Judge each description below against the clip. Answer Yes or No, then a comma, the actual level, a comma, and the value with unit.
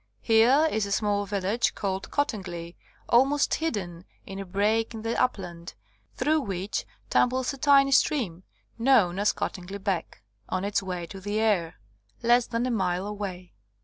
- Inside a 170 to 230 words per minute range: No, average, 155 wpm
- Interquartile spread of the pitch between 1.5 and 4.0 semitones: No, average, 4.4 semitones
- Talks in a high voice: Yes, high, 205 Hz